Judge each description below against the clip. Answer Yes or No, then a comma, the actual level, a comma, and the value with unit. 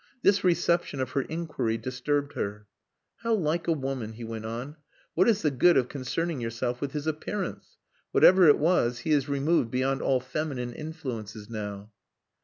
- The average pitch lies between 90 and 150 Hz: Yes, low, 135 Hz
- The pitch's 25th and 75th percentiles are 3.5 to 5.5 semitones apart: Yes, average, 5.1 semitones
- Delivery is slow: No, average, 170 wpm